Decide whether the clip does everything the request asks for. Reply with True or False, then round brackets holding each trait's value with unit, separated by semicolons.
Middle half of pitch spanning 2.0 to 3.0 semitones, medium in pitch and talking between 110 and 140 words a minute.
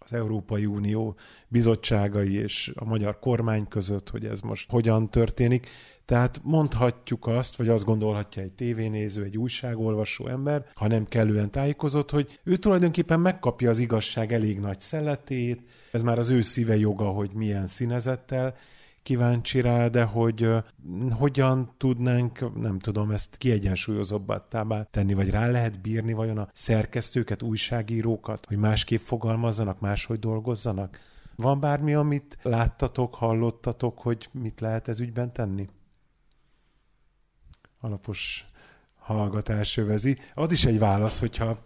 False (2.7 semitones; 115 Hz; 130 wpm)